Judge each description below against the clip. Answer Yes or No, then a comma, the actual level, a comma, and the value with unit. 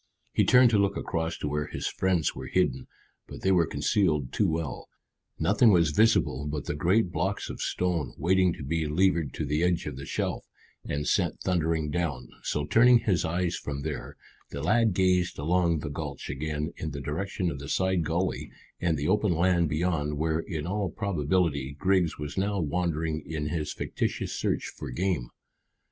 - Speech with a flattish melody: No, average, 3.8 semitones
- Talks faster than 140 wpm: Yes, average, 185 wpm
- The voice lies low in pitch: Yes, very low, 80 Hz